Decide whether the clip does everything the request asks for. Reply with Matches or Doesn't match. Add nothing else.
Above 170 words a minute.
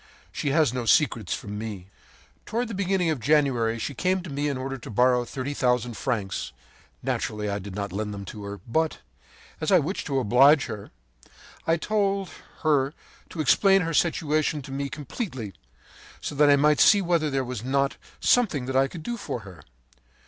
Matches